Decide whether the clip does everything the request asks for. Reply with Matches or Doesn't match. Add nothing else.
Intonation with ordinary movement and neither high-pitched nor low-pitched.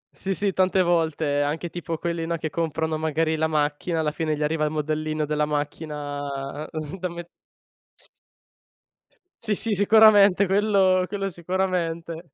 Matches